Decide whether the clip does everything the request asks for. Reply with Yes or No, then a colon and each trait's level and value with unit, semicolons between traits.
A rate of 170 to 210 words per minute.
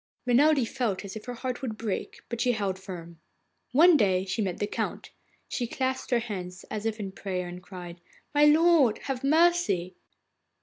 Yes: average, 180 wpm